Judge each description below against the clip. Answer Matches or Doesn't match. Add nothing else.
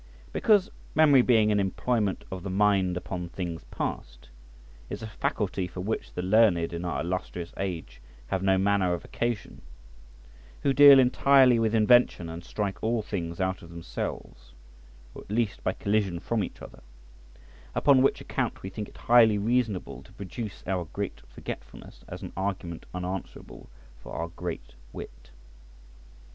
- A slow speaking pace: Doesn't match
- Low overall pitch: Matches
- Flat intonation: Doesn't match